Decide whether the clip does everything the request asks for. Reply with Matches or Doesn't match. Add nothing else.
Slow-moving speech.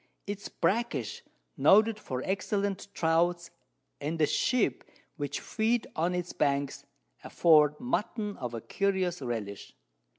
Matches